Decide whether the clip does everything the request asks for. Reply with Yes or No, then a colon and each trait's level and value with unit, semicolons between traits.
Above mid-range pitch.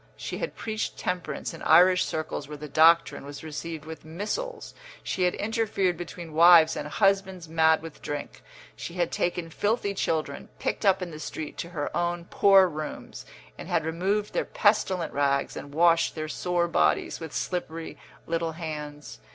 No: medium, 170 Hz